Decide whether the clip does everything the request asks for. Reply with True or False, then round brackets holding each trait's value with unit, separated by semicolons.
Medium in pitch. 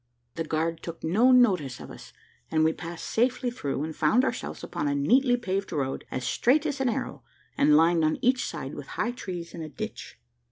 True (170 Hz)